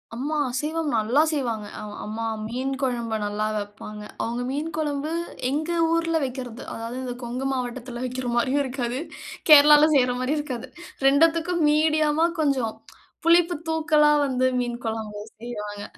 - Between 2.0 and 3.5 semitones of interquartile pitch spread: No, average, 4.2 semitones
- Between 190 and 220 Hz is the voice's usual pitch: No, very high, 260 Hz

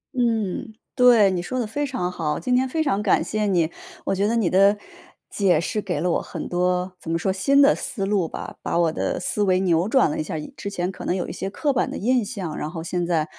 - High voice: Yes, high, 195 Hz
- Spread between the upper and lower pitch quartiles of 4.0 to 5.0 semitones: Yes, average, 4.6 semitones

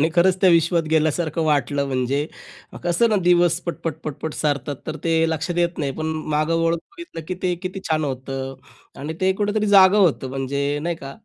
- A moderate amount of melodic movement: Yes, average, 3.6 semitones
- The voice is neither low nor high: Yes, medium, 160 Hz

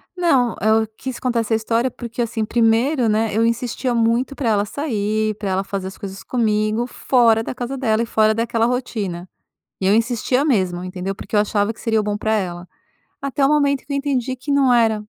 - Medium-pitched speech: No, high, 225 Hz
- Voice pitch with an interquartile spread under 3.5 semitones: Yes, average, 2.9 semitones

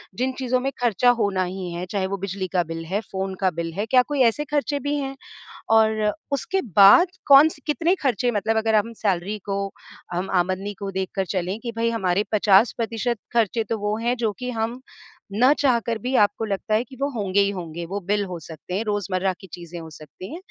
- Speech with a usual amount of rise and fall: Yes, average, 4.2 semitones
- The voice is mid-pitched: No, high, 210 Hz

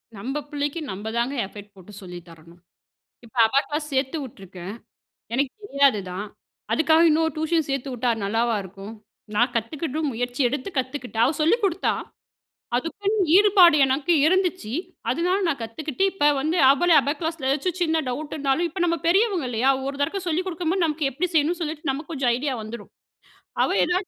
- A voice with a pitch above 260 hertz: Yes, very high, 285 Hz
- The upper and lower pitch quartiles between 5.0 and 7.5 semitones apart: Yes, wide, 5.5 semitones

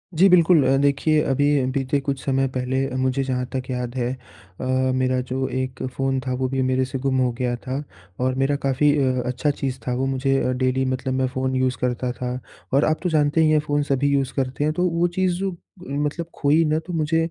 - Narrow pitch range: Yes, narrow, 2.2 semitones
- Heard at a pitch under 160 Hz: Yes, low, 135 Hz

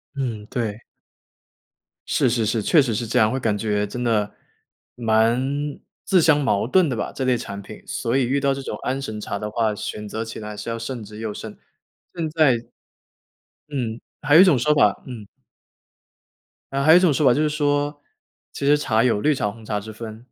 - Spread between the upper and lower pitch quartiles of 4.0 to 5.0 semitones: Yes, average, 4.4 semitones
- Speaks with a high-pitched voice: No, low, 120 Hz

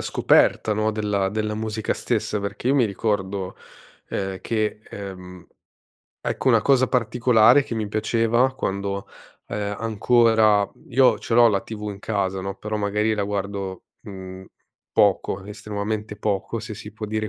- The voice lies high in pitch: No, low, 105 Hz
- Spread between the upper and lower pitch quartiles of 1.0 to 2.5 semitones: Yes, narrow, 2.0 semitones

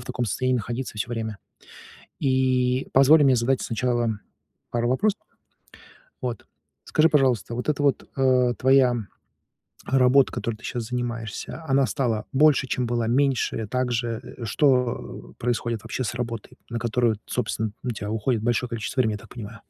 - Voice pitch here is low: Yes, low, 125 Hz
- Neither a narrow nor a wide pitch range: No, narrow, 2.3 semitones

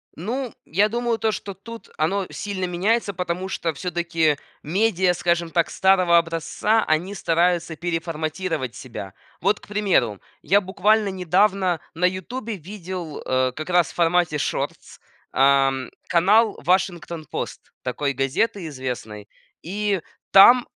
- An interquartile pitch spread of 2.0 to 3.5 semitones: No, average, 4.0 semitones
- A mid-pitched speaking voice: Yes, medium, 180 Hz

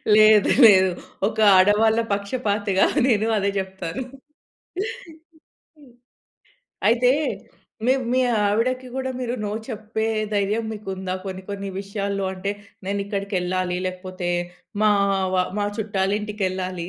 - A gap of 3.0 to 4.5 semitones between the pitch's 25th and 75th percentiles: No, narrow, 2.4 semitones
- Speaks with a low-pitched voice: No, high, 200 Hz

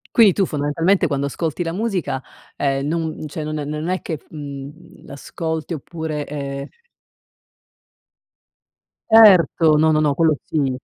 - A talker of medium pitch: Yes, medium, 155 Hz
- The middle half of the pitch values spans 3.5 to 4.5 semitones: No, average, 2.8 semitones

